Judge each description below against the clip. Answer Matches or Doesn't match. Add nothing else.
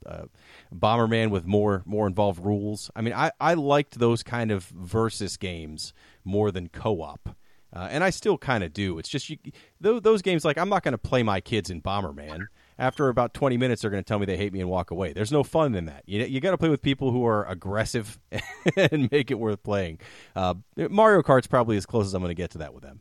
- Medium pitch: Doesn't match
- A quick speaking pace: Matches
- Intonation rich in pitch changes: Matches